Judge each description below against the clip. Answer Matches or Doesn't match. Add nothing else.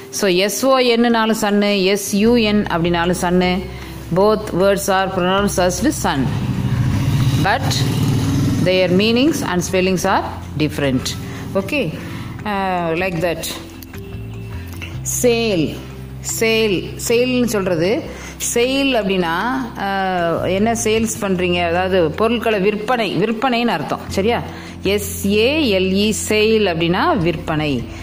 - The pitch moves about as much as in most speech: Doesn't match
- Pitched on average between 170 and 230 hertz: Matches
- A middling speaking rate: Doesn't match